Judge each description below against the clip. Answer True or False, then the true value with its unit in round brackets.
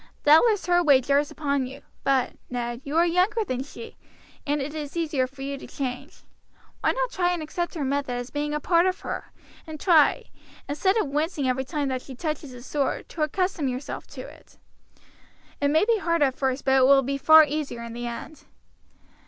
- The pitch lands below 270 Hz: False (290 Hz)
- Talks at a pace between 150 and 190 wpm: False (205 wpm)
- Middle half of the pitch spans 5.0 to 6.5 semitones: False (3.9 semitones)